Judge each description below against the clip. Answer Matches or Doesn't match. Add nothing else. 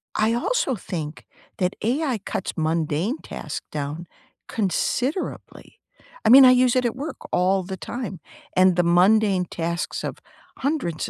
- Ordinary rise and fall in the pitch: Doesn't match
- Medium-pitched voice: Doesn't match